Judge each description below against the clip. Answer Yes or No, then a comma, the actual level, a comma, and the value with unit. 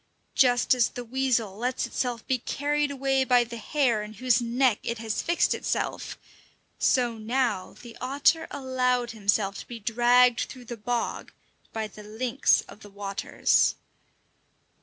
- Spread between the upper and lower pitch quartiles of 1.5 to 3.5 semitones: Yes, average, 2.7 semitones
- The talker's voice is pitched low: No, high, 245 Hz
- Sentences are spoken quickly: No, average, 150 wpm